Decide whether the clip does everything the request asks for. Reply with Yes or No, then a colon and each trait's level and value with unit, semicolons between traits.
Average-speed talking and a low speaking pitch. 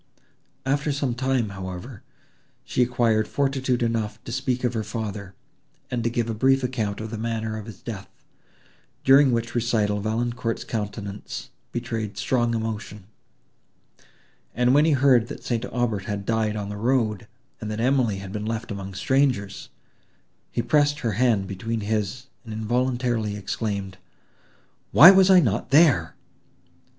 Yes: average, 150 wpm; low, 115 Hz